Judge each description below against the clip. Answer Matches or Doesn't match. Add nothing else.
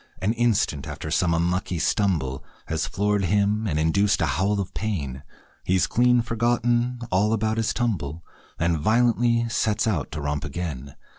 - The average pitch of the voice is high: Doesn't match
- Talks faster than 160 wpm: Doesn't match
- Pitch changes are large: Matches